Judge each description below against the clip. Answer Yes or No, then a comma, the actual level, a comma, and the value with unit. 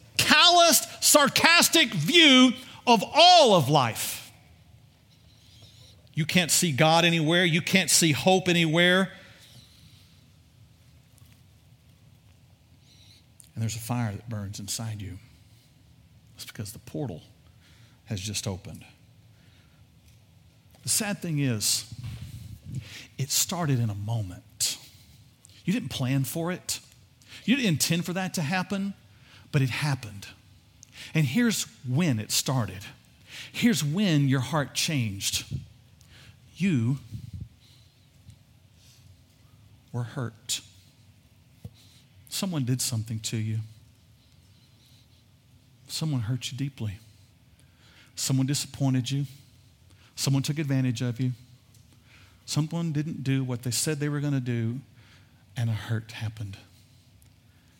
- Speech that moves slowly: Yes, slow, 105 wpm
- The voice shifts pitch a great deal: No, average, 4.1 semitones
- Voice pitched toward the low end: Yes, low, 120 Hz